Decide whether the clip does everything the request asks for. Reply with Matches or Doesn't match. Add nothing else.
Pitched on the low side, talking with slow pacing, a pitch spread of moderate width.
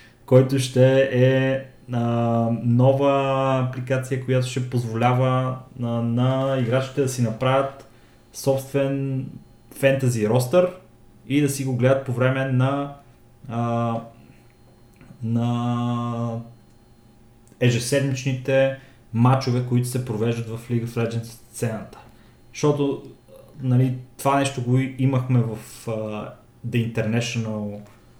Doesn't match